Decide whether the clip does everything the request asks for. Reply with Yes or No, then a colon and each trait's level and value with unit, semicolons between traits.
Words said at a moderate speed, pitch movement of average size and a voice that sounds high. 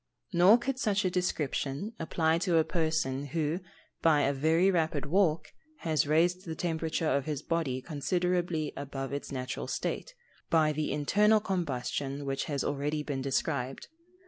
No: average, 150 wpm; average, 3.7 semitones; medium, 155 Hz